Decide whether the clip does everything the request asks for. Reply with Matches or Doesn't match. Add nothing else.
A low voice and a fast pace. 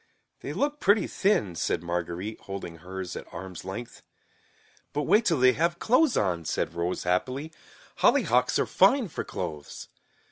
Doesn't match